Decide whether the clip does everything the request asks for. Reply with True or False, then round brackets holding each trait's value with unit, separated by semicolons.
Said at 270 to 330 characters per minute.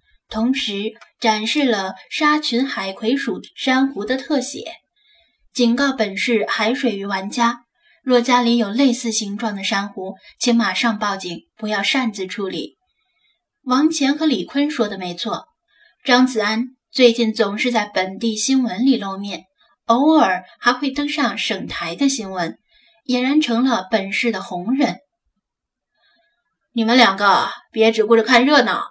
False (210 characters per minute)